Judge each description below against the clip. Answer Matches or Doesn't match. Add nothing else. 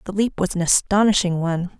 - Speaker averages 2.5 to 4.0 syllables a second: Doesn't match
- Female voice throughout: Matches